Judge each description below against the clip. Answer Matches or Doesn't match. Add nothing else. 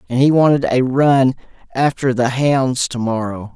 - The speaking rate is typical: Matches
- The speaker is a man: Matches